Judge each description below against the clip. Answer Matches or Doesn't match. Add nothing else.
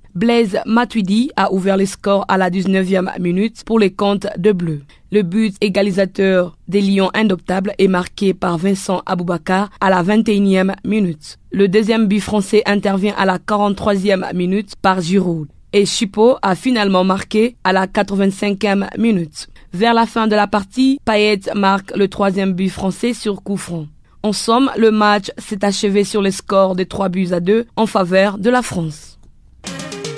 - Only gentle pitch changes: Matches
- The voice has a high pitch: Matches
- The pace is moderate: Matches